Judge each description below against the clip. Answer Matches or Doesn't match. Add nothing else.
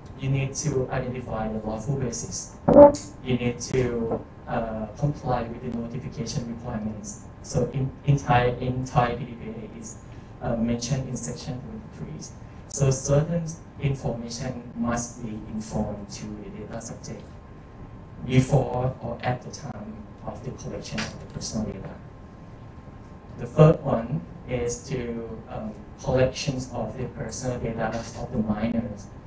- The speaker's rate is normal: Doesn't match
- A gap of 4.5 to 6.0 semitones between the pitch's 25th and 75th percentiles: Doesn't match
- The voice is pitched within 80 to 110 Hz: Doesn't match